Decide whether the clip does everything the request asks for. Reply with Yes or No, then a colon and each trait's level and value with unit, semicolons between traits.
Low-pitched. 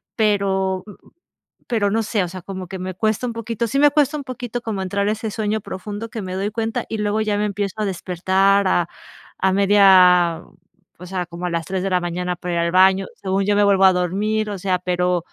No: high, 195 Hz